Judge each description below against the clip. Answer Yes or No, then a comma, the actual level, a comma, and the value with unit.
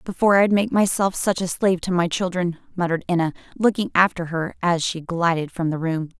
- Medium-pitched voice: Yes, medium, 180 Hz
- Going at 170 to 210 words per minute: Yes, fast, 205 wpm